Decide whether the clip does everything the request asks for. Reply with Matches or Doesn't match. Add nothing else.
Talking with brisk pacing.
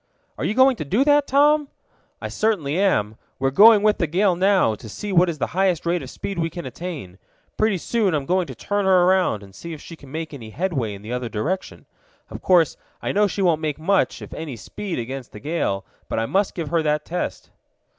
Matches